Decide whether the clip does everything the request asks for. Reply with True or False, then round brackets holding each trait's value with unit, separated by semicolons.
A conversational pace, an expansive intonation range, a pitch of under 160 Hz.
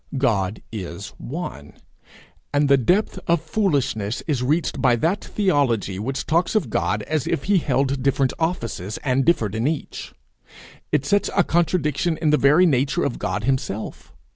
True (160 wpm; 6.0 semitones; 140 Hz)